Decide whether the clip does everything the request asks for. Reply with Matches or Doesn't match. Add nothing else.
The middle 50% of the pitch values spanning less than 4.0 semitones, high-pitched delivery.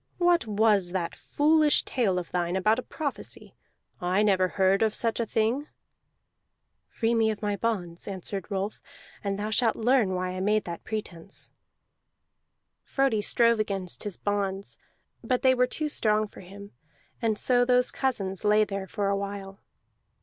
Matches